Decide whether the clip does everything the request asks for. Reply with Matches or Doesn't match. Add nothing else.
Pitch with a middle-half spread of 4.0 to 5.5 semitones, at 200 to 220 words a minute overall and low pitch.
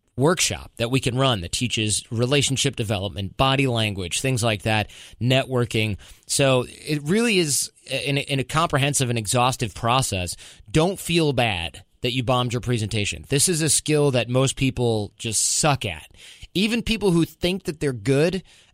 Doesn't match